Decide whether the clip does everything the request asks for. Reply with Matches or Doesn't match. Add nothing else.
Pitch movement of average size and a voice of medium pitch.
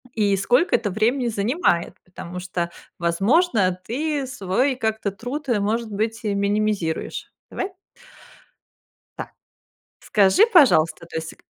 Doesn't match